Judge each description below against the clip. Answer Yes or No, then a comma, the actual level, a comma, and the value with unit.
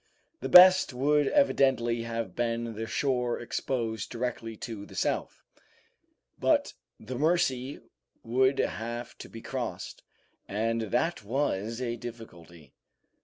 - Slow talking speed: Yes, slow, 120 wpm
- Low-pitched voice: Yes, low, 120 Hz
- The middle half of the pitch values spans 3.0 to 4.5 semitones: No, narrow, 2.6 semitones